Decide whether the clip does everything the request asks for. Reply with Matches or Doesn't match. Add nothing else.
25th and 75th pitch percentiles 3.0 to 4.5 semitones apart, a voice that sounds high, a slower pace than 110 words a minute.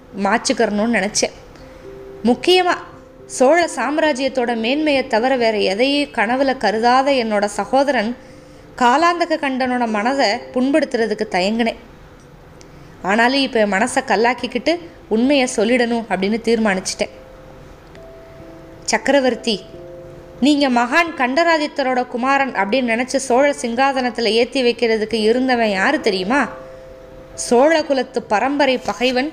Matches